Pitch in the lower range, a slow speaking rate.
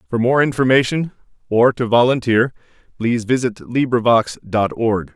Yes: low, 120 Hz; slow, 130 wpm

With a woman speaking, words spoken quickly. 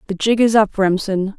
Yes: female; fast, 215 wpm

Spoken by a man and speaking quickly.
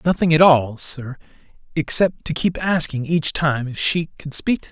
No: male; average, 190 wpm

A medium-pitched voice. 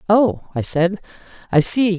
No: high, 195 Hz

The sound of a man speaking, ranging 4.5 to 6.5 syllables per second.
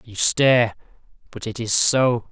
No: male; 4.2 syllables/s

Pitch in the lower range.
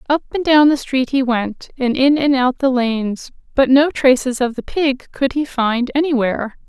No: very high, 265 Hz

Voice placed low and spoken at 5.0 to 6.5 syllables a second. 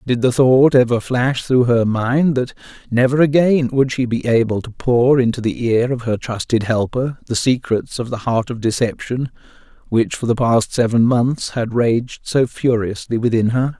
No: low, 120 Hz; 4.5 syllables/s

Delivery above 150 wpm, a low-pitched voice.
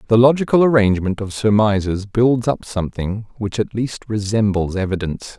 No: average, 145 wpm; low, 105 Hz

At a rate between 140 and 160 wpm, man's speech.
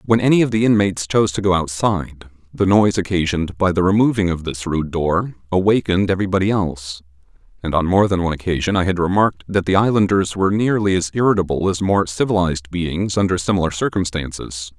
No: average, 185 wpm; male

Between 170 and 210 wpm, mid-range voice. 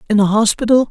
No: average, 200 wpm; high, 220 Hz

